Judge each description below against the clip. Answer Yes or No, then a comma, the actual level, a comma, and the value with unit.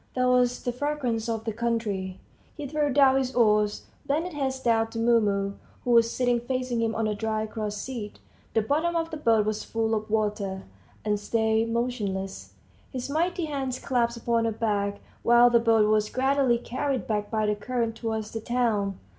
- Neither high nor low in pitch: No, high, 230 Hz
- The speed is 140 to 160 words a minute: No, average, 190 wpm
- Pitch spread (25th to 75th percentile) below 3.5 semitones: Yes, average, 2.9 semitones